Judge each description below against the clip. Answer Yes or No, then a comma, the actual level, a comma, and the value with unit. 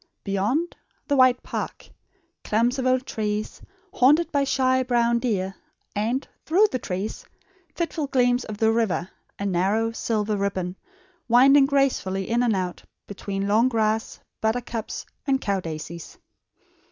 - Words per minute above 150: No, slow, 135 wpm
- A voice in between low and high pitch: No, high, 225 Hz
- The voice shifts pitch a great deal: No, average, 4.3 semitones